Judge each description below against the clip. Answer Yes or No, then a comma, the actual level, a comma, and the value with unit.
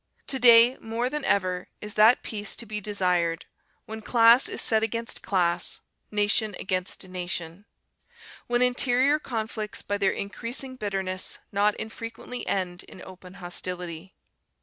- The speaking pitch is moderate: No, high, 210 Hz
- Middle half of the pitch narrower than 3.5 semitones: No, average, 3.9 semitones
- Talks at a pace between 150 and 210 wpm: No, slow, 135 wpm